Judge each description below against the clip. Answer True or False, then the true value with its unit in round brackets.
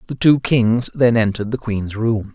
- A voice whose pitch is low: True (115 Hz)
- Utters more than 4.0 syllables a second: True (4.7 syllables/s)